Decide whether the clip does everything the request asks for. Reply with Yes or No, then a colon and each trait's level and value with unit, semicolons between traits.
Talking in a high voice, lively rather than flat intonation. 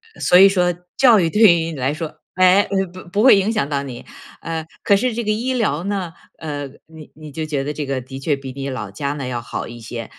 No: medium, 160 Hz; wide, 6.0 semitones